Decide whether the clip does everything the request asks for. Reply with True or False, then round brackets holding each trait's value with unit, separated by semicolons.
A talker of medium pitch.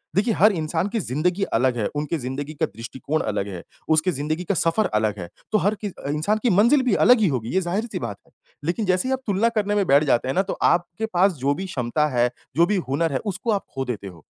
True (165 Hz)